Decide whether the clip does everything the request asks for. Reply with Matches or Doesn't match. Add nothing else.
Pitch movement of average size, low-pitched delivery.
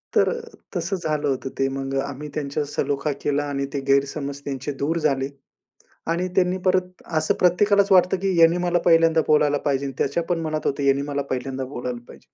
Doesn't match